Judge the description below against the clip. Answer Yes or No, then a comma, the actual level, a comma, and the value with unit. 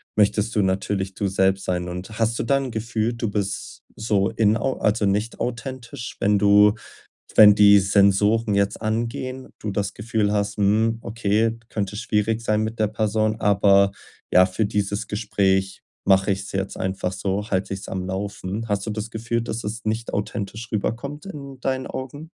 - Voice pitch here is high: No, low, 105 Hz